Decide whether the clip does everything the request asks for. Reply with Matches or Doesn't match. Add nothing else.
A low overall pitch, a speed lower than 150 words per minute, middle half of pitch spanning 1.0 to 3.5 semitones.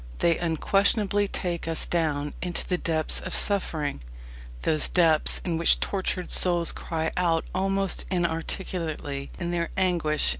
Doesn't match